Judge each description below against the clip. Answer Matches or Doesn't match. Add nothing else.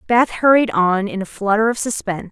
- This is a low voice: Doesn't match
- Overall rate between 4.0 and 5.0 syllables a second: Doesn't match